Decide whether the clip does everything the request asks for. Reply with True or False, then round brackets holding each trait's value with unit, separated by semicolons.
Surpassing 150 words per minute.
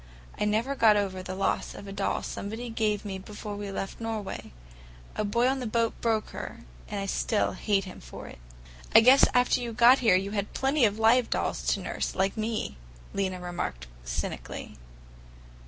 True (190 wpm)